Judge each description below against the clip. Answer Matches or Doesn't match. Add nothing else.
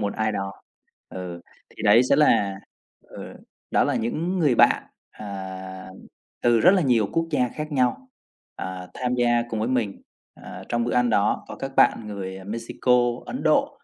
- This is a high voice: Doesn't match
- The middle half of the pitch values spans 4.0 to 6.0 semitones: Matches